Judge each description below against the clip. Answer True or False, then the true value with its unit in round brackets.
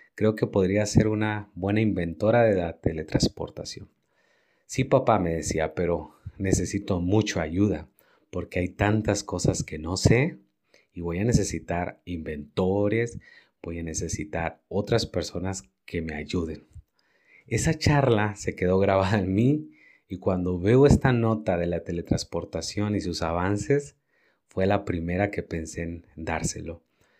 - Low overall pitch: True (95 Hz)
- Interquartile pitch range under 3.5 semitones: False (4.1 semitones)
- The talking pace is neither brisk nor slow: True (140 wpm)